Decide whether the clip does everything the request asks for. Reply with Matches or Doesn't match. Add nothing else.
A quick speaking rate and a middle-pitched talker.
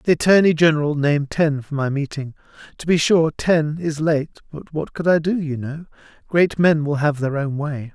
Matches